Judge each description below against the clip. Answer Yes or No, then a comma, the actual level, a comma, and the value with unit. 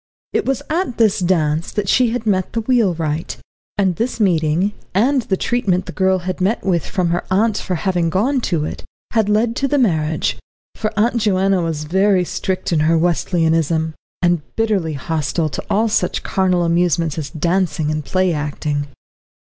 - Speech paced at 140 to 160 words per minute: No, average, 175 wpm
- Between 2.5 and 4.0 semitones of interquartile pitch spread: No, average, 4.5 semitones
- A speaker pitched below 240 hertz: Yes, medium, 185 Hz